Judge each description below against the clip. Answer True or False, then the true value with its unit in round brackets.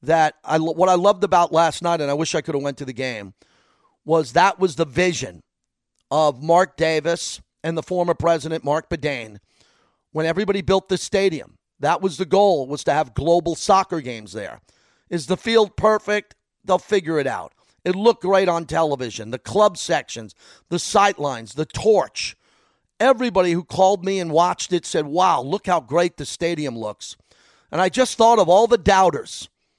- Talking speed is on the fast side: False (185 wpm)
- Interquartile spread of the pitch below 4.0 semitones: False (4.4 semitones)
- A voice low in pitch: False (170 Hz)